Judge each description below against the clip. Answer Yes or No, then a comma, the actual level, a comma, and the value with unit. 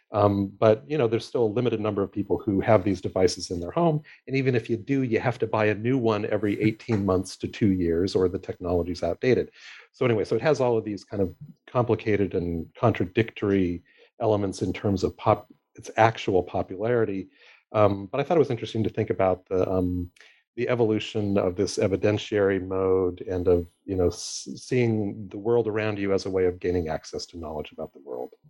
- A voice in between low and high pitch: No, low, 105 Hz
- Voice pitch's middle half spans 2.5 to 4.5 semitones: Yes, average, 3.3 semitones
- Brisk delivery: Yes, fast, 210 wpm